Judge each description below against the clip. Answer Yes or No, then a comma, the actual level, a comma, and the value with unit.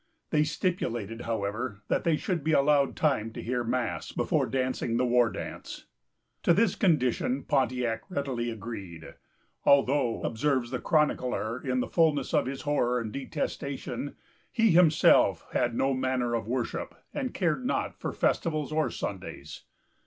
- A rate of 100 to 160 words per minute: Yes, average, 145 wpm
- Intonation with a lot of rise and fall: No, average, 4.3 semitones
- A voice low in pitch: Yes, low, 130 Hz